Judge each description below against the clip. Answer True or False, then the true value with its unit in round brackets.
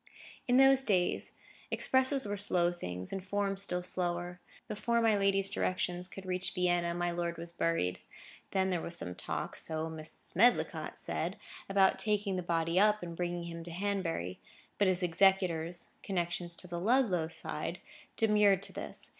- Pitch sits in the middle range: True (180 Hz)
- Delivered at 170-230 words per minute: False (155 wpm)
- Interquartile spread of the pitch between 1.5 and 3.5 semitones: True (2.7 semitones)